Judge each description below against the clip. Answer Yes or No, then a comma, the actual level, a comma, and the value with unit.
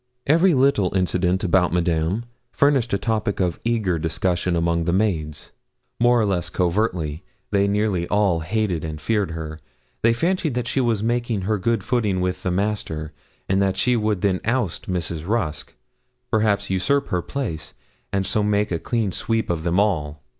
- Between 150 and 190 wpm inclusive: Yes, average, 170 wpm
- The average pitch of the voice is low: Yes, low, 100 Hz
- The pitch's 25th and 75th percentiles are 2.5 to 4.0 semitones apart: No, average, 4.5 semitones